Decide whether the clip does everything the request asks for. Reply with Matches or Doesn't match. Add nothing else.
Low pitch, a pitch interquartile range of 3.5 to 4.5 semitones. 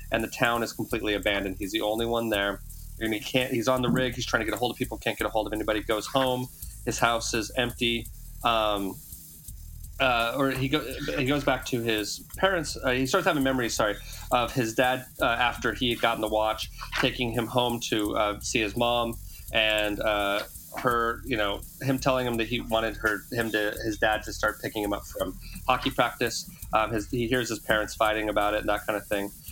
Doesn't match